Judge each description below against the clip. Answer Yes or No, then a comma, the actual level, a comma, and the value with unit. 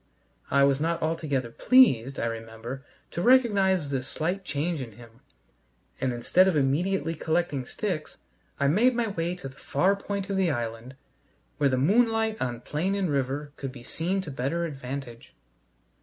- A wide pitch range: Yes, wide, 6.2 semitones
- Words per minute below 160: No, average, 165 wpm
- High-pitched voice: No, medium, 150 Hz